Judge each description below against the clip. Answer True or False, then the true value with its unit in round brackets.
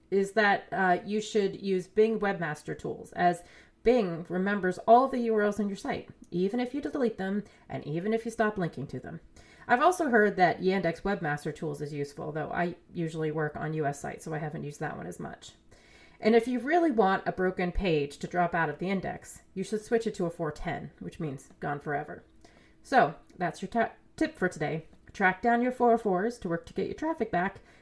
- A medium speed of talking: False (210 wpm)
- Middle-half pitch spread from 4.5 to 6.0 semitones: True (4.8 semitones)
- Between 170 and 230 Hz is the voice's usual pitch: True (185 Hz)